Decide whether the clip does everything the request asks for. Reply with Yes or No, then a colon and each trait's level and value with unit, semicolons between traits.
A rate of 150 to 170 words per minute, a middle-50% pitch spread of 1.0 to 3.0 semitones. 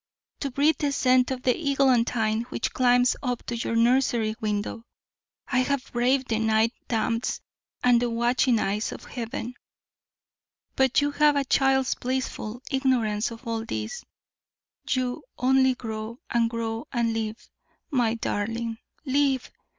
No: average, 140 wpm; narrow, 2.6 semitones